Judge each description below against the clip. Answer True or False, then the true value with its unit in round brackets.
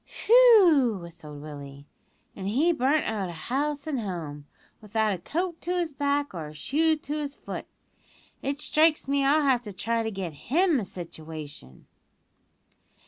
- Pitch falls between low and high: False (240 Hz)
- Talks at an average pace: True (160 wpm)